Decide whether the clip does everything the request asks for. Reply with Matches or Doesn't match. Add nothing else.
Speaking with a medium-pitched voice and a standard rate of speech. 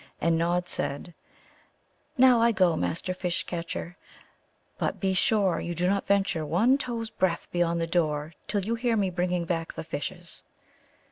Matches